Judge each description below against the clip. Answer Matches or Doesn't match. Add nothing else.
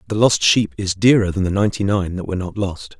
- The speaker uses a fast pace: Matches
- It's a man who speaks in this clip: Matches